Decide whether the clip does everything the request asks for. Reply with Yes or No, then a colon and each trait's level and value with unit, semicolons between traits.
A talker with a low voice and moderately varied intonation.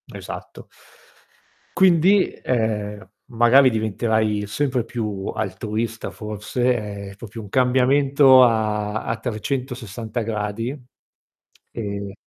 Yes: low, 110 Hz; average, 3.3 semitones